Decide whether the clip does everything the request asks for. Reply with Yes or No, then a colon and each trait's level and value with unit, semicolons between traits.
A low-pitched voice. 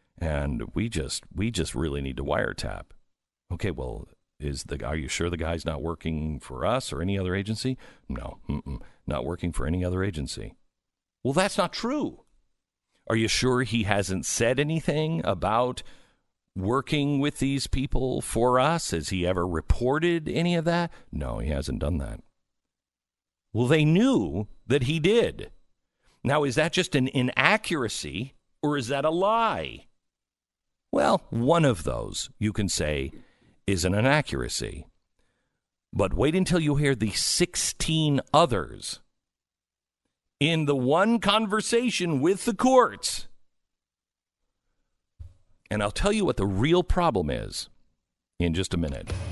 Yes: low, 120 Hz